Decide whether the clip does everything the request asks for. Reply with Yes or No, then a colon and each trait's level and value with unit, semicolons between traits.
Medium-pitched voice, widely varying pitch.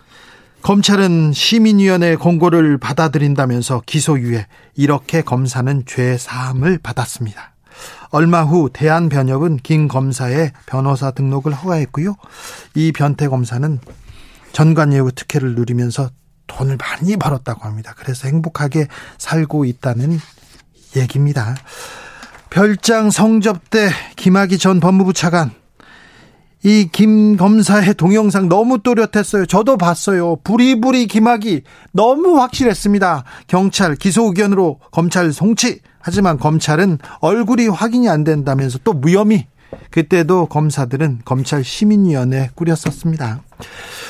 Yes: medium, 160 Hz; wide, 6.5 semitones